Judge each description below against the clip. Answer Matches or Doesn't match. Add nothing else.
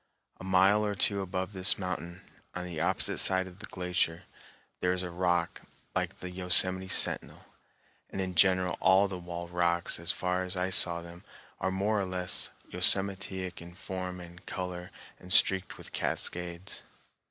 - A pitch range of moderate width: Doesn't match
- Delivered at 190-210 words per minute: Doesn't match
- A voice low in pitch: Matches